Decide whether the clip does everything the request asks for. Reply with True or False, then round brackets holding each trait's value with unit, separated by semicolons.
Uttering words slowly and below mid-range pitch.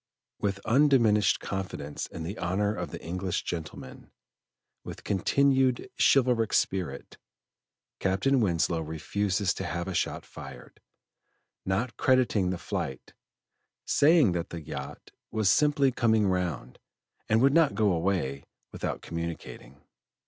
True (120 wpm; 100 Hz)